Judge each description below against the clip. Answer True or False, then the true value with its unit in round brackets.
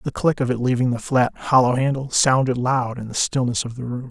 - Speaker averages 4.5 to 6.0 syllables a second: True (5.5 syllables/s)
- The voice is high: False (125 Hz)